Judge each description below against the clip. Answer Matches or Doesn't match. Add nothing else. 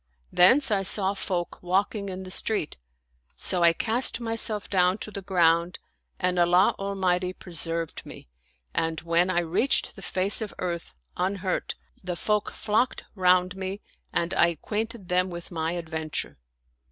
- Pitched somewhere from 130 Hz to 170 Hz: Doesn't match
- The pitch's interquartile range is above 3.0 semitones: Doesn't match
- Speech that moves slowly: Doesn't match